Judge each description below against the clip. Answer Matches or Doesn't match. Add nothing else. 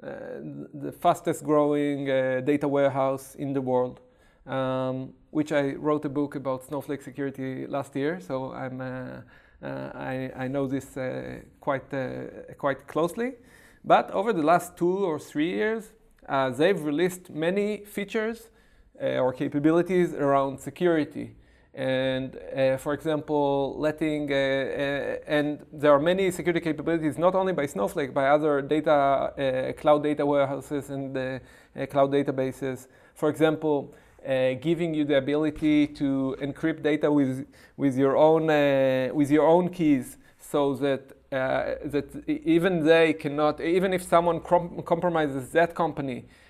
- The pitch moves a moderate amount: Matches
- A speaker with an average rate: Matches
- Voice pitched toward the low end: Doesn't match